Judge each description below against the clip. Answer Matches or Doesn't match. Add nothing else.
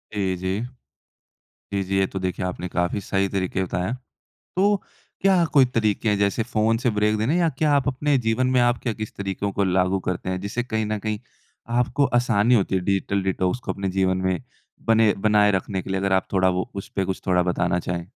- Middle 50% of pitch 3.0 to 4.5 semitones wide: Matches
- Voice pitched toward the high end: Doesn't match